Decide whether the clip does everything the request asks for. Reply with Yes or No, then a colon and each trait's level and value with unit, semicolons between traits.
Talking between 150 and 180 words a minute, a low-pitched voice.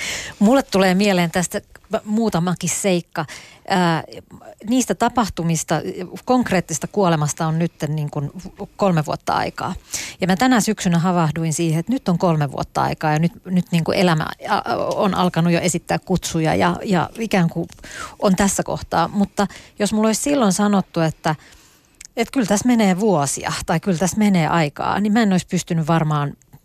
No: fast, 155 wpm; medium, 185 Hz